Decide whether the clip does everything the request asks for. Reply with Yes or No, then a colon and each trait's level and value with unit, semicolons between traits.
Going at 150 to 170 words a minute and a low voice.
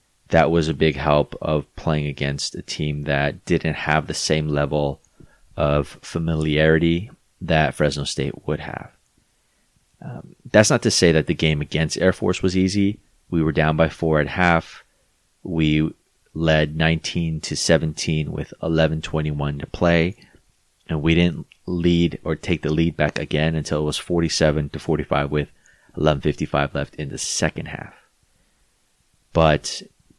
Yes: average, 155 wpm; very low, 80 Hz